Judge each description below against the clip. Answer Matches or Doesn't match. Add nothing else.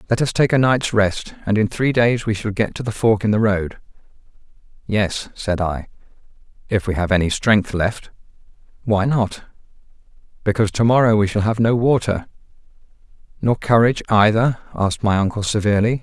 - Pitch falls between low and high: Doesn't match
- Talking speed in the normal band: Matches